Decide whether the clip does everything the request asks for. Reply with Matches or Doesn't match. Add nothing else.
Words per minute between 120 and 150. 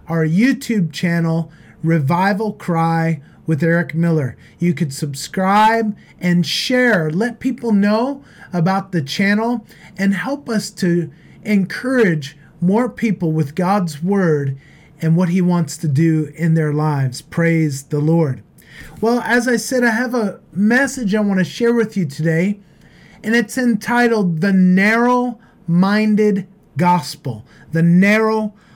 Matches